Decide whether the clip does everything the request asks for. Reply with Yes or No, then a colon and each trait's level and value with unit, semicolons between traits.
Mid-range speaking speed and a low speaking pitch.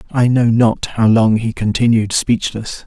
Yes: average, 165 wpm; low, 115 Hz